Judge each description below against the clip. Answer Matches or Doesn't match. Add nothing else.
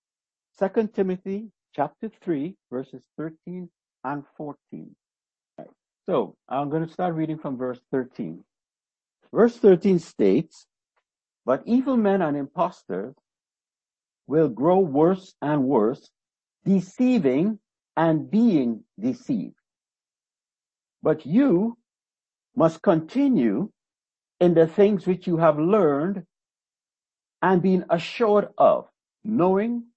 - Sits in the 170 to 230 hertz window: Matches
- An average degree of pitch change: Doesn't match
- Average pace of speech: Doesn't match